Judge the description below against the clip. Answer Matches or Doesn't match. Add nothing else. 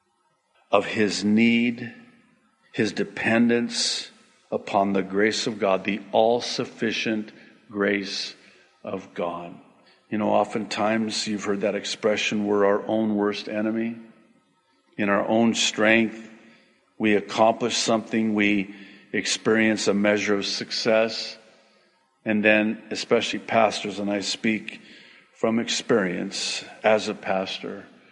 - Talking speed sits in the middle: Doesn't match